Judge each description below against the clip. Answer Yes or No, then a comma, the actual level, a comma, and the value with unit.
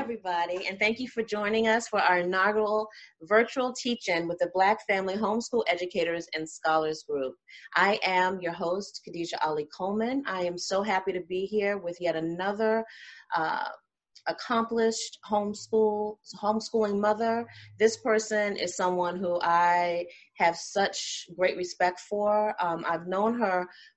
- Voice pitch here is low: No, high, 195 Hz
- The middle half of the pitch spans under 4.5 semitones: Yes, average, 3.7 semitones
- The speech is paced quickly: No, average, 145 wpm